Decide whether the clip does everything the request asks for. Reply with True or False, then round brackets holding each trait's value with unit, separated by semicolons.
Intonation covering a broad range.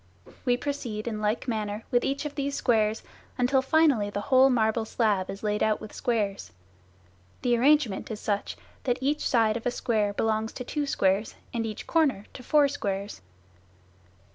False (4.0 semitones)